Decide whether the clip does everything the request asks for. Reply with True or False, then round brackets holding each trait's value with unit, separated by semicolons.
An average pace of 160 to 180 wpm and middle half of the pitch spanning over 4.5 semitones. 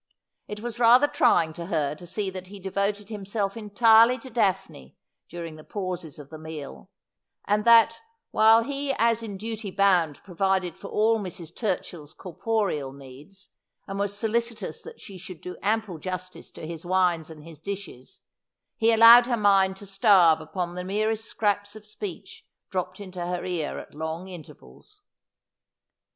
False (165 wpm; 4.2 semitones)